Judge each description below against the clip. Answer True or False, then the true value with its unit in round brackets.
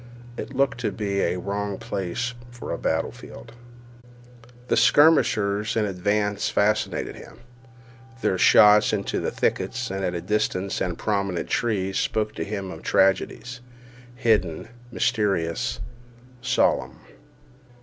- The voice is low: True (105 Hz)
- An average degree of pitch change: True (3.7 semitones)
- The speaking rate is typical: False (115 wpm)